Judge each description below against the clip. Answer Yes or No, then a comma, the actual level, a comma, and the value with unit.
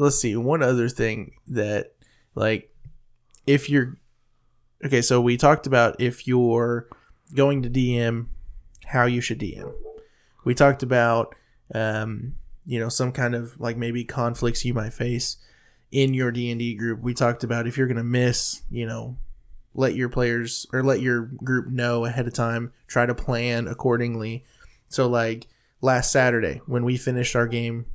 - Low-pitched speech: Yes, low, 120 Hz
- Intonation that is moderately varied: No, narrow, 1.5 semitones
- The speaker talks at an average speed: Yes, average, 160 wpm